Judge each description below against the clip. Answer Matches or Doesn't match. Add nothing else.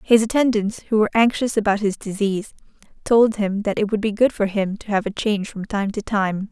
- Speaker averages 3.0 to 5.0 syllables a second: Doesn't match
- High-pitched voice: Matches